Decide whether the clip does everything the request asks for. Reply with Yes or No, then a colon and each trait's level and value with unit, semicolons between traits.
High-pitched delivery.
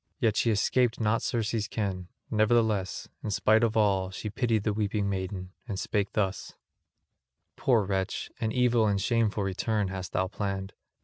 No: low, 105 Hz